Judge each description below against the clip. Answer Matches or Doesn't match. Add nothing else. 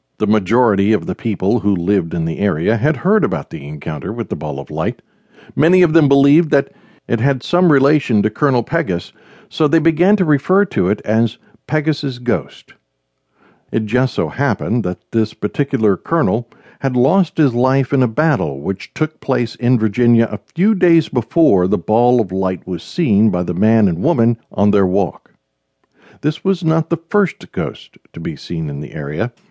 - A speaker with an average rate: Matches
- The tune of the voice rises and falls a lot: Matches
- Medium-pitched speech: Doesn't match